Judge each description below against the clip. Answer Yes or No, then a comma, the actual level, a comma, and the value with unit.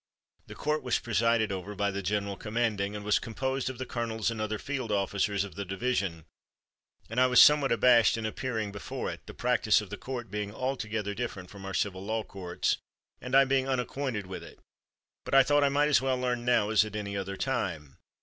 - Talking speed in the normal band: No, fast, 210 wpm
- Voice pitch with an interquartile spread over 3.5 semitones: Yes, average, 4.0 semitones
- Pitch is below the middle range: Yes, low, 110 Hz